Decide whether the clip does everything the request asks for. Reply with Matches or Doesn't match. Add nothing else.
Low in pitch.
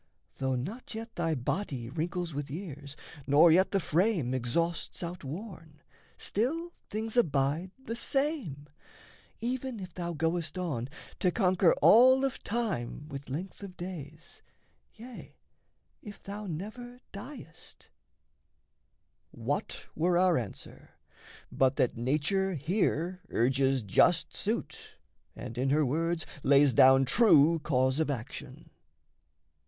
Doesn't match